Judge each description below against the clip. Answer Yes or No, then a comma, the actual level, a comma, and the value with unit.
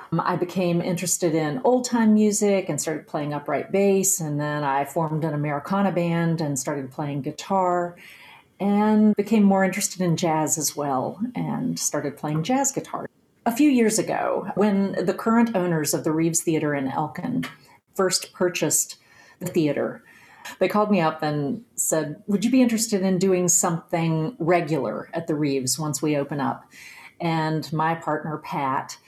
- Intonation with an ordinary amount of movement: Yes, average, 4.2 semitones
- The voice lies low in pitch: No, medium, 170 Hz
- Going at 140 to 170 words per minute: Yes, average, 165 wpm